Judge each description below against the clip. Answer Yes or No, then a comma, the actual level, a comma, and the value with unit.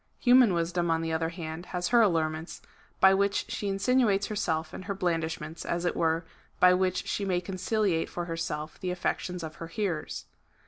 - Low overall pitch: No, medium, 175 Hz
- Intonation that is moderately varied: Yes, average, 3.0 semitones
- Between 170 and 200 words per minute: Yes, average, 180 wpm